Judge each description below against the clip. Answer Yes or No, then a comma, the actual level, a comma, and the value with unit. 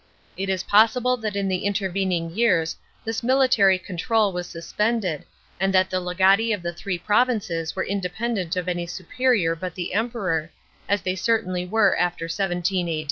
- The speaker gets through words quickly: No, average, 165 wpm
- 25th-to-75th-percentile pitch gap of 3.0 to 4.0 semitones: Yes, average, 3.5 semitones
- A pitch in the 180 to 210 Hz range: Yes, high, 190 Hz